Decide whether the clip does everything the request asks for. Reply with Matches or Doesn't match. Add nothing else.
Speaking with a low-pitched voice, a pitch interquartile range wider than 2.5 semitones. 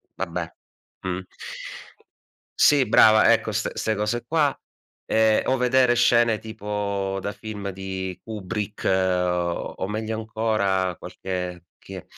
Matches